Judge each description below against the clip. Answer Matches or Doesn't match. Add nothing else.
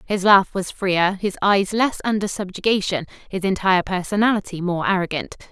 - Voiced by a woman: Matches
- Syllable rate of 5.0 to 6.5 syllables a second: Matches